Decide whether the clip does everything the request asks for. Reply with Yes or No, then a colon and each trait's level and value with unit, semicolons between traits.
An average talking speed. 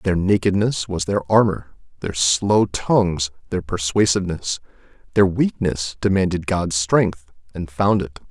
No: slow, 130 wpm